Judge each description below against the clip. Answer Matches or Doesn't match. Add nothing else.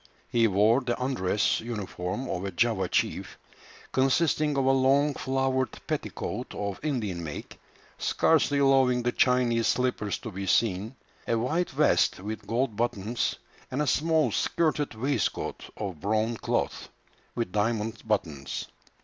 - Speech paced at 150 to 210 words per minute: Doesn't match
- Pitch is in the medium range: Doesn't match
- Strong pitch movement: Doesn't match